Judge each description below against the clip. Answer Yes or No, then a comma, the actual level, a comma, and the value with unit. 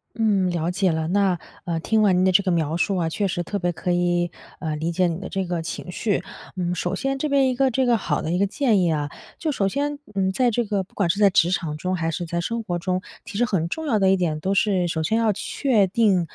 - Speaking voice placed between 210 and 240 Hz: No, high, 190 Hz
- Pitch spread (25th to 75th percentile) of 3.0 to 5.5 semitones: Yes, average, 3.7 semitones